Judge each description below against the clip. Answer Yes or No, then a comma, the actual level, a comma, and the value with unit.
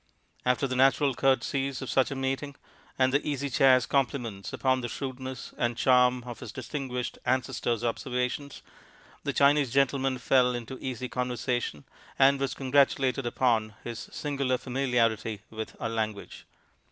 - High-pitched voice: No, low, 130 Hz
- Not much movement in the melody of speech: Yes, narrow, 2.0 semitones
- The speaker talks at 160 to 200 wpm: No, average, 140 wpm